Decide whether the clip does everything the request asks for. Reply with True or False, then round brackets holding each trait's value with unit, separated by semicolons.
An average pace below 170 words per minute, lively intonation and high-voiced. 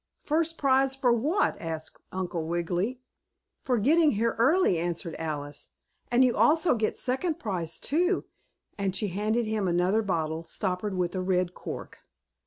True (150 wpm; 7.0 semitones; 210 Hz)